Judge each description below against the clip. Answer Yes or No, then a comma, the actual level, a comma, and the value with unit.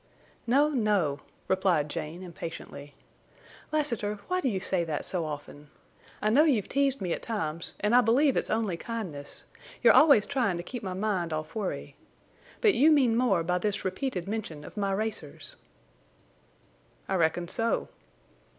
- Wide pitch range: Yes, wide, 6.1 semitones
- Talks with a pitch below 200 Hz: No, high, 205 Hz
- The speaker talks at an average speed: Yes, average, 160 wpm